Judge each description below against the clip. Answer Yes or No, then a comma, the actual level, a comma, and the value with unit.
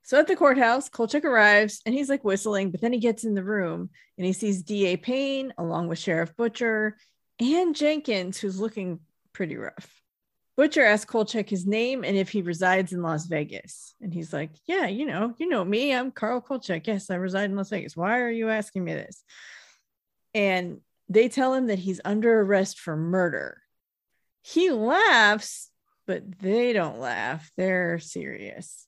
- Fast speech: No, average, 180 wpm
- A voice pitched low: No, high, 210 Hz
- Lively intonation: No, average, 4.6 semitones